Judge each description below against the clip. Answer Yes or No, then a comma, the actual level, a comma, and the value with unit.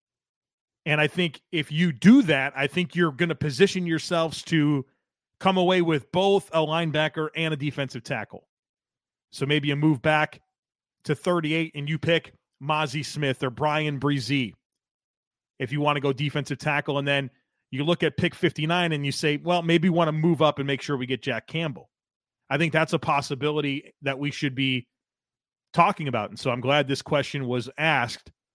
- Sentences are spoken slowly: No, average, 190 wpm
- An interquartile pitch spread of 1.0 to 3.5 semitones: Yes, average, 2.8 semitones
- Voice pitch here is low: No, medium, 150 Hz